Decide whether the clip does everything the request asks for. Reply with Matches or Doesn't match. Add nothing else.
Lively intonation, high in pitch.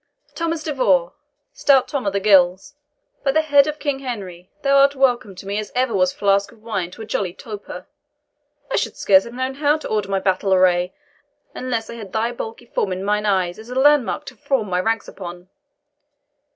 Matches